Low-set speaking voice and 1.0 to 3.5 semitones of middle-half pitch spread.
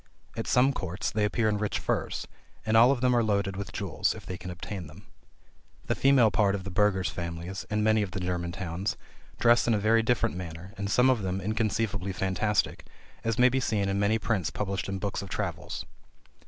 Yes: low, 100 Hz; average, 2.9 semitones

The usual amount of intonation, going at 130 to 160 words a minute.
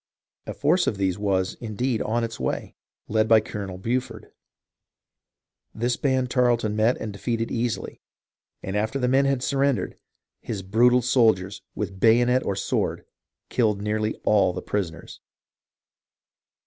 Yes: average, 3.3 semitones; slow, 135 wpm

